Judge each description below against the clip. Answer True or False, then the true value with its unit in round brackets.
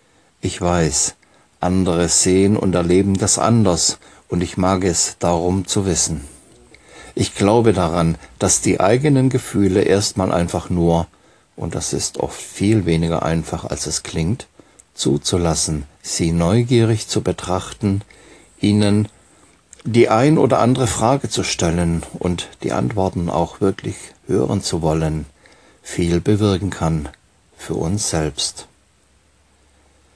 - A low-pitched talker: True (90 Hz)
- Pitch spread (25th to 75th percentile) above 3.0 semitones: True (3.7 semitones)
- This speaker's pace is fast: False (125 wpm)